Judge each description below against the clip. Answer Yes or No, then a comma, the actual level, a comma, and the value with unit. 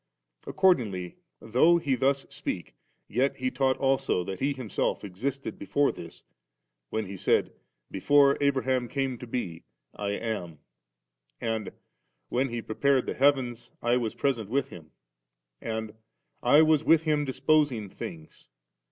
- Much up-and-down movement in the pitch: No, average, 4.5 semitones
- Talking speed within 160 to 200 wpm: No, average, 145 wpm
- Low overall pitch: Yes, low, 125 Hz